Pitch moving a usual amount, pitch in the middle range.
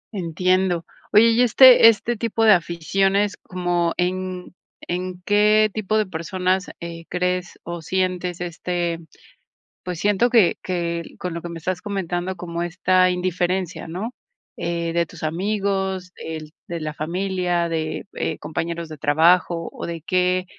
No: narrow, 2.0 semitones; medium, 180 Hz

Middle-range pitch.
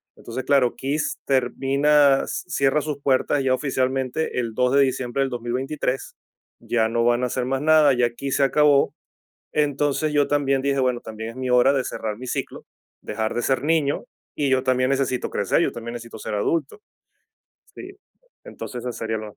No: low, 130 Hz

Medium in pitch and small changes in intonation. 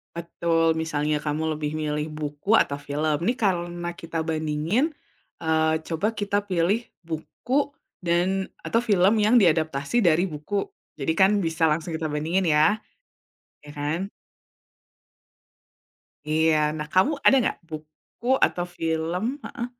No: medium, 165 Hz; average, 3.7 semitones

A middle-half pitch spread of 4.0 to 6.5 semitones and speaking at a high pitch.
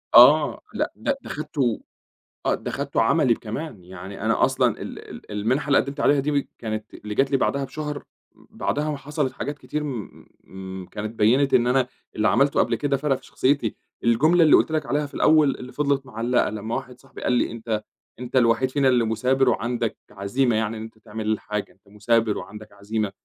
No: average, 4.4 semitones; low, 125 Hz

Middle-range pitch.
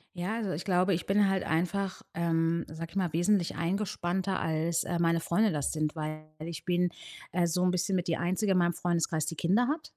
Yes: medium, 175 Hz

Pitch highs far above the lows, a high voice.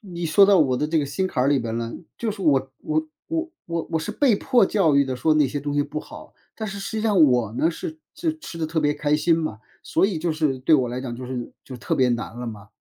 No: wide, 6.9 semitones; medium, 155 Hz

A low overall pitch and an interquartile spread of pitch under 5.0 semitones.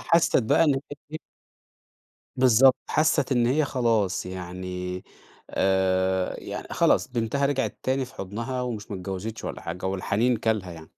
No: low, 110 Hz; wide, 5.6 semitones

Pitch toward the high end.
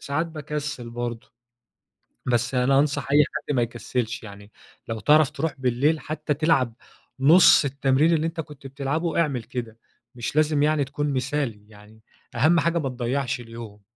No: low, 135 Hz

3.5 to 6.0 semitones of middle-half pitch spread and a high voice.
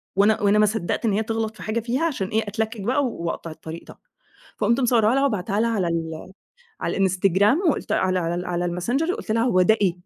Yes: average, 4.1 semitones; high, 210 Hz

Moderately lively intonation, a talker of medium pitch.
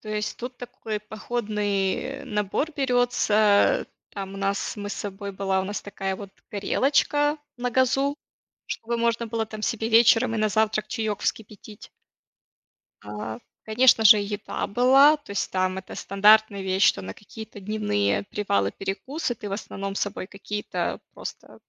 No: average, 3.0 semitones; high, 210 Hz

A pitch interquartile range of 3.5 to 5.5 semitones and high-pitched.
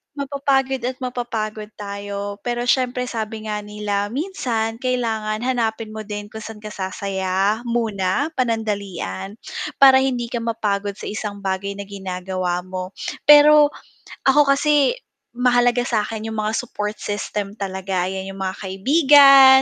Yes: average, 3.9 semitones; high, 215 Hz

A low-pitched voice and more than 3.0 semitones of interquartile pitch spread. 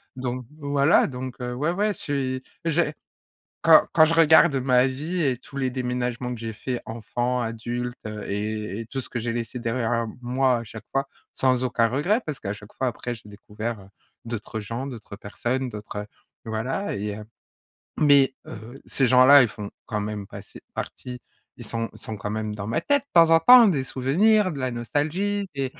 Yes: low, 125 Hz; average, 3.6 semitones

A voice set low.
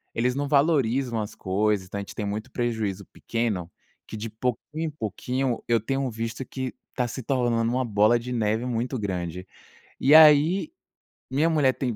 Yes: low, 120 Hz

